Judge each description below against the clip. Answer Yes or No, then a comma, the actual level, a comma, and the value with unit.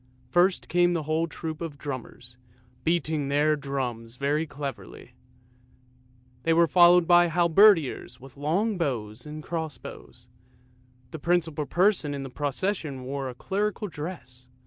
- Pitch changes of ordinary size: Yes, average, 4.1 semitones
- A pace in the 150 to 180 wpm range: No, slow, 135 wpm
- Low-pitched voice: No, medium, 155 Hz